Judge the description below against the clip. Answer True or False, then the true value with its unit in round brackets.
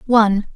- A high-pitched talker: True (215 Hz)